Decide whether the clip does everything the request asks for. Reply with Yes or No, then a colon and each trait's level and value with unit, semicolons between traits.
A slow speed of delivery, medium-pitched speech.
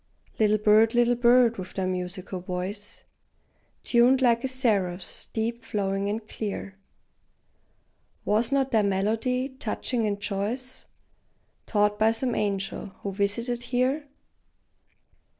No: slow, 115 wpm; high, 220 Hz